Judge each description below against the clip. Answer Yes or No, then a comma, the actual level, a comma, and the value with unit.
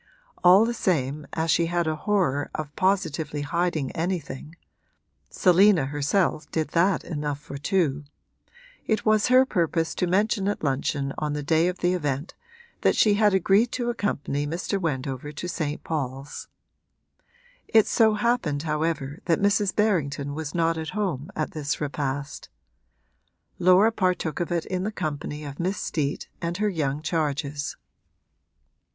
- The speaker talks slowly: No, average, 150 wpm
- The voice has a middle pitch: Yes, medium, 165 Hz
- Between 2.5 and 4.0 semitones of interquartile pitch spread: No, average, 4.5 semitones